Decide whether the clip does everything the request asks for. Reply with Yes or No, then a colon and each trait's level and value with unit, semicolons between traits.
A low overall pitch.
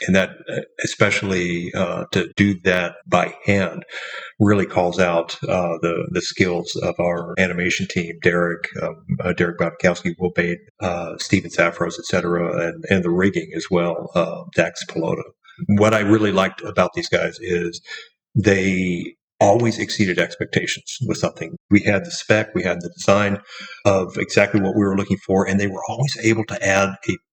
Yes: very low, 95 Hz